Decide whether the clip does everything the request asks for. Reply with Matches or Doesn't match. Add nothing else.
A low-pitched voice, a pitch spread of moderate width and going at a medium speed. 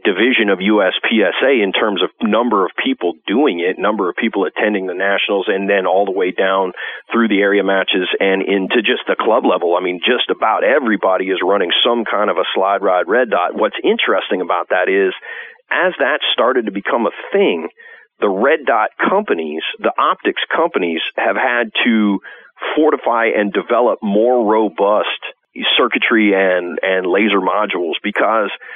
Matches